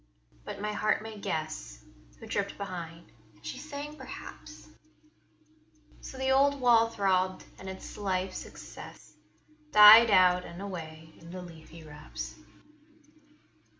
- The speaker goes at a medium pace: No, slow, 125 wpm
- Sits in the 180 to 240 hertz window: Yes, high, 190 Hz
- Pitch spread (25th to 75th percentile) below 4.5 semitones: No, average, 5.3 semitones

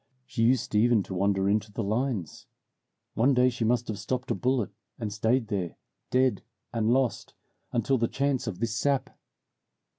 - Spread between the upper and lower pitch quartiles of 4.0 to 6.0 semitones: No, average, 3.4 semitones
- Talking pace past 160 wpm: Yes, average, 170 wpm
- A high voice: No, low, 115 Hz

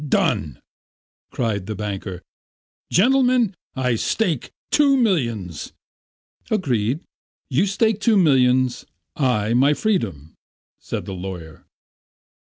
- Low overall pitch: Yes, low, 125 Hz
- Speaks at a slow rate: Yes, slow, 95 wpm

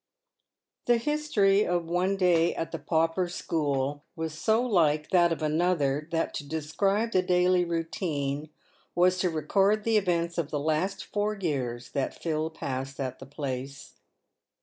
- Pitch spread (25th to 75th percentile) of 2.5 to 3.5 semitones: No, average, 3.9 semitones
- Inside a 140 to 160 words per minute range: Yes, average, 150 wpm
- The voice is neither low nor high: Yes, medium, 165 Hz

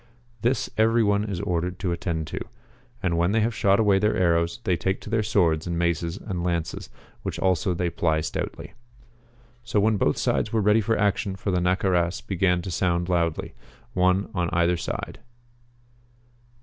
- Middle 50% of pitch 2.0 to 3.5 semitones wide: Yes, average, 2.9 semitones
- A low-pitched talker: Yes, very low, 90 Hz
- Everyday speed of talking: Yes, average, 175 wpm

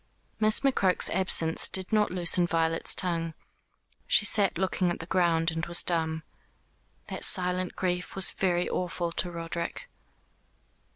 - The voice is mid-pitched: Yes, medium, 175 Hz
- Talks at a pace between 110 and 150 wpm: Yes, slow, 135 wpm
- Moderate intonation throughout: No, narrow, 2.0 semitones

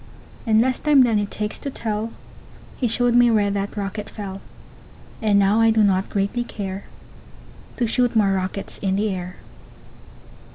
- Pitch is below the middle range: No, high, 210 Hz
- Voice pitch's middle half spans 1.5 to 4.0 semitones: Yes, narrow, 2.6 semitones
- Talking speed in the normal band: Yes, average, 165 wpm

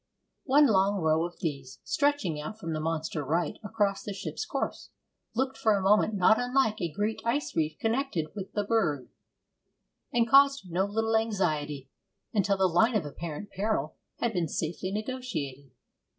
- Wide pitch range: Yes, wide, 5.7 semitones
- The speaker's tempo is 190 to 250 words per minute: No, average, 165 wpm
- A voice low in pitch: No, high, 195 Hz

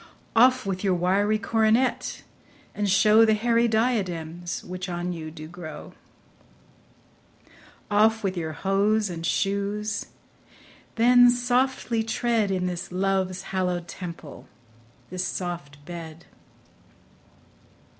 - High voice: Yes, high, 195 Hz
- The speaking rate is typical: No, slow, 105 wpm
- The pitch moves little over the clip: No, average, 4.0 semitones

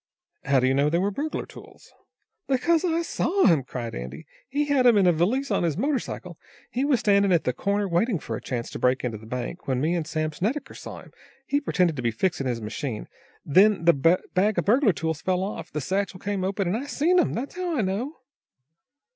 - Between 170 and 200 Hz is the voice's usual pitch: Yes, medium, 185 Hz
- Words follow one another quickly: Yes, fast, 230 wpm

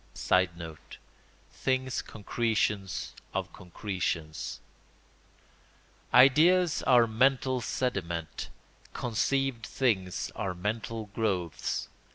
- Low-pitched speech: Yes, low, 110 Hz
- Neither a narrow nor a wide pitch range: No, wide, 5.8 semitones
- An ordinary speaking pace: No, slow, 70 wpm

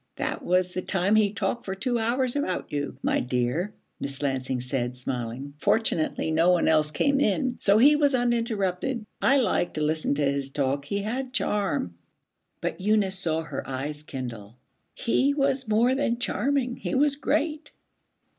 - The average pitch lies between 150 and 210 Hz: Yes, high, 190 Hz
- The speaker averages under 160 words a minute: No, average, 165 wpm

